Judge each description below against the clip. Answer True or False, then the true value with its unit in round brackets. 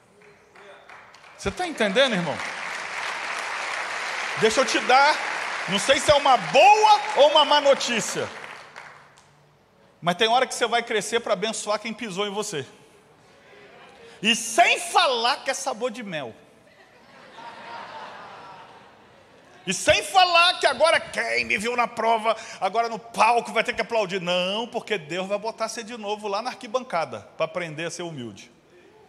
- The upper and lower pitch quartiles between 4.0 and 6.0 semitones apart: True (4.6 semitones)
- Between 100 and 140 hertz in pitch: False (230 Hz)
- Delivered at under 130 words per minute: False (150 wpm)